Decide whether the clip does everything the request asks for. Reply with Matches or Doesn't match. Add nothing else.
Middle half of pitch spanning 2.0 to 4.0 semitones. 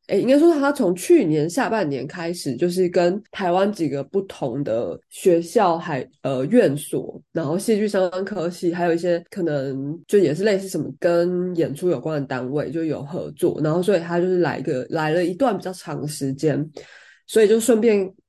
Matches